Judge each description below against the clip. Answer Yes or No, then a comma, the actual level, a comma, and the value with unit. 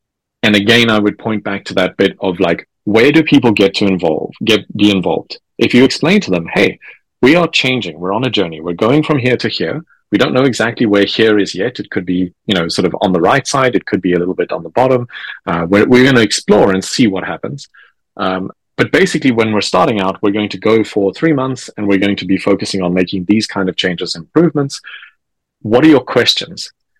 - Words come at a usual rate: No, fast, 240 wpm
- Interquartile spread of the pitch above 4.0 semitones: Yes, average, 4.6 semitones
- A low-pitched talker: Yes, low, 105 Hz